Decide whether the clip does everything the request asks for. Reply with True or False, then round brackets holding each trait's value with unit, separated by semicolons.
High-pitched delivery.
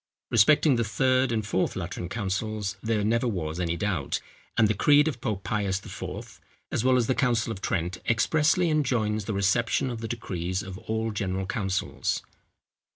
False (110 Hz)